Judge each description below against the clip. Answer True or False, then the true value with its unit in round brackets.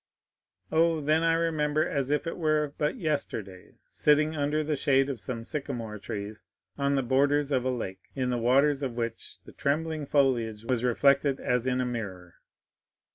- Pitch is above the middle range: False (140 Hz)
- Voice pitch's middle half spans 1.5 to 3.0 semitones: False (3.8 semitones)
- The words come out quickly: False (175 wpm)